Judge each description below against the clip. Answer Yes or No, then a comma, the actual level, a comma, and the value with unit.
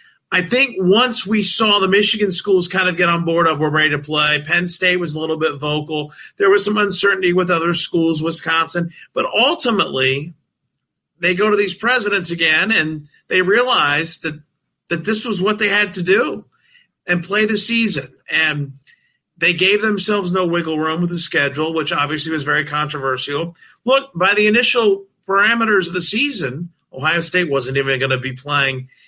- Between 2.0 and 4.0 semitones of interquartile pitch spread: No, average, 4.7 semitones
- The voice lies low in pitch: No, medium, 175 Hz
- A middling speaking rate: Yes, average, 180 wpm